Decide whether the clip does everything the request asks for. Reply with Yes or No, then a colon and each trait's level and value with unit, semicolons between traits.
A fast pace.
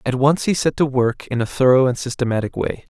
Yes: fast, 245 wpm